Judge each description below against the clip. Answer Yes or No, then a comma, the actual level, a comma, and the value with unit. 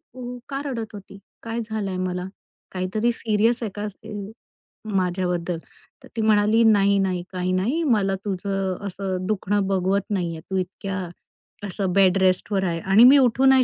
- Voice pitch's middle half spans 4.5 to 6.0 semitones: No, average, 2.8 semitones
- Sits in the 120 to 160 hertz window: No, high, 195 Hz